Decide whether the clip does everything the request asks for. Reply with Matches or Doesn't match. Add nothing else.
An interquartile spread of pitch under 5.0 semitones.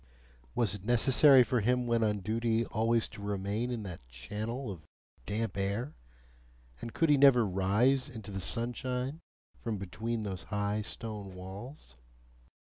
Matches